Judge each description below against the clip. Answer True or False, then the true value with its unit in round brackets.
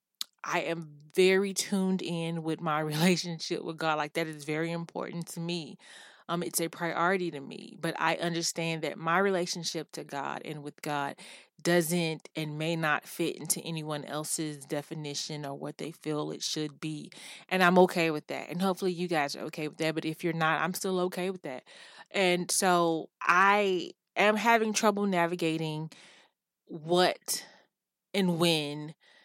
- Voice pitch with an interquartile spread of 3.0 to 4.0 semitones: False (2.4 semitones)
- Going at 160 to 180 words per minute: True (170 wpm)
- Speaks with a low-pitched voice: False (165 Hz)